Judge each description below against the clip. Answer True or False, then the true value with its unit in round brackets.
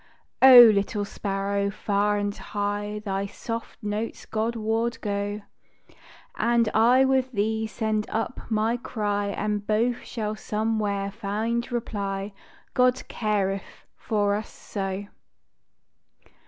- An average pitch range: False (2.0 semitones)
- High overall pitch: True (210 Hz)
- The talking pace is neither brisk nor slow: False (115 wpm)